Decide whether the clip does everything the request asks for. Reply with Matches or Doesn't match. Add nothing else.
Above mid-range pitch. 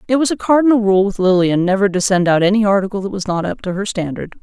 Matches